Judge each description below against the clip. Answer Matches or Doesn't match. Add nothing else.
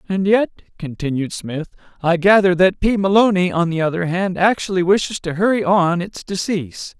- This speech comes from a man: Matches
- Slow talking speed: Doesn't match